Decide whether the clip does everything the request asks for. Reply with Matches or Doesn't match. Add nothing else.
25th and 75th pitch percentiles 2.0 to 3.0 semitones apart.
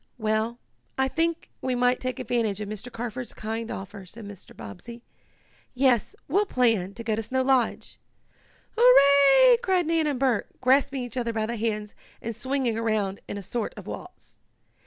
Doesn't match